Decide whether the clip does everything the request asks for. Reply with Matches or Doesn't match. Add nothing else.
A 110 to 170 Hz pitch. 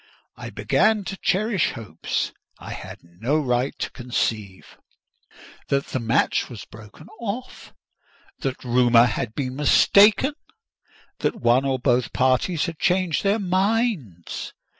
Matches